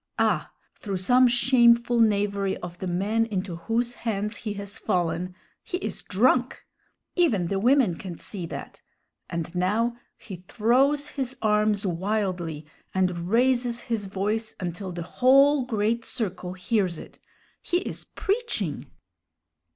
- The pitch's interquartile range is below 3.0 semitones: No, average, 4.6 semitones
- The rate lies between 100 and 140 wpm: Yes, slow, 135 wpm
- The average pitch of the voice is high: Yes, high, 210 Hz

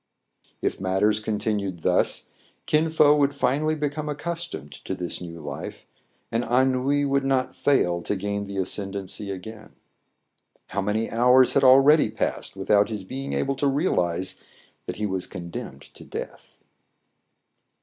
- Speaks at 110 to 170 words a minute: Yes, average, 140 wpm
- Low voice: Yes, low, 110 Hz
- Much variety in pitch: Yes, wide, 6.3 semitones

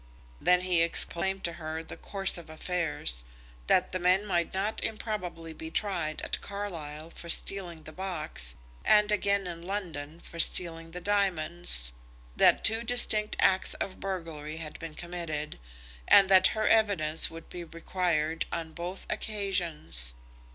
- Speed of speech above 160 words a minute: No, average, 145 wpm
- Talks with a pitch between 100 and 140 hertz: No, medium, 175 Hz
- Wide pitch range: No, average, 3.3 semitones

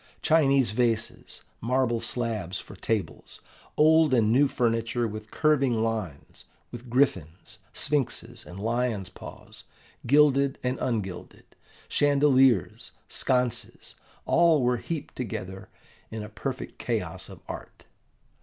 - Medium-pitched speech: No, low, 120 Hz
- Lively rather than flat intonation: No, average, 3.9 semitones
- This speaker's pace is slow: Yes, slow, 110 wpm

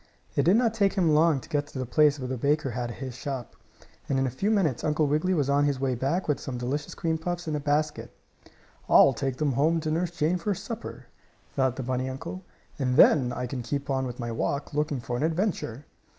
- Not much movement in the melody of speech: No, average, 3.7 semitones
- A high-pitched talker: No, medium, 145 Hz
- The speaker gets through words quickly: Yes, fast, 235 wpm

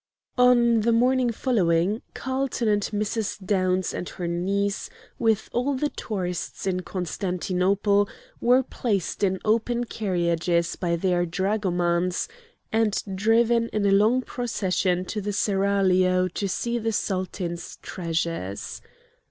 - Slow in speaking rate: Yes, slow, 120 wpm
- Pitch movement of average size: Yes, average, 3.8 semitones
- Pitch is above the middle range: Yes, high, 200 Hz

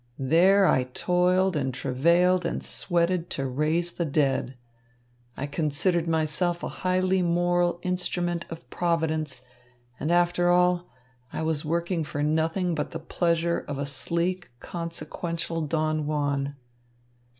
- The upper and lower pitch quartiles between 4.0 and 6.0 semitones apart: No, narrow, 2.6 semitones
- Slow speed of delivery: Yes, slow, 130 wpm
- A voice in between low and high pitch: Yes, medium, 170 Hz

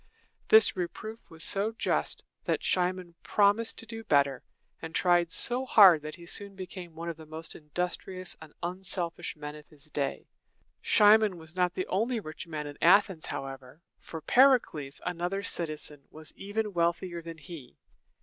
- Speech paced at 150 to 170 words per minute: Yes, average, 165 wpm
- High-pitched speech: No, medium, 175 Hz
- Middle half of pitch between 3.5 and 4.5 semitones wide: Yes, average, 4.0 semitones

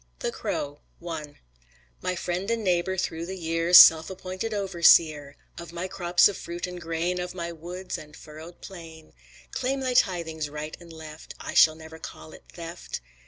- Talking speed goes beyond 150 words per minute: Yes, average, 170 wpm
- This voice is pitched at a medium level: Yes, medium, 170 Hz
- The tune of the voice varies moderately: No, narrow, 2.3 semitones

